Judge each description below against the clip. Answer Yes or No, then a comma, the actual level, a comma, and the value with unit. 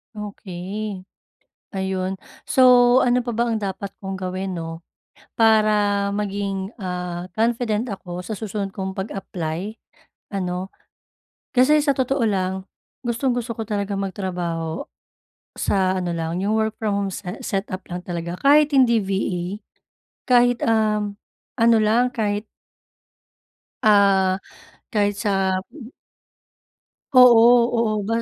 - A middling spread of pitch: Yes, average, 3.3 semitones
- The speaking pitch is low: No, high, 200 Hz